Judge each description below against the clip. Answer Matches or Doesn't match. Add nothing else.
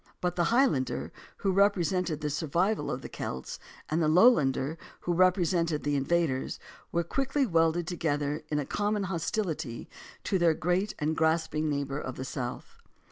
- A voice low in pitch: Doesn't match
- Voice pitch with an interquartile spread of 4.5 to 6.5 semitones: Doesn't match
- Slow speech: Doesn't match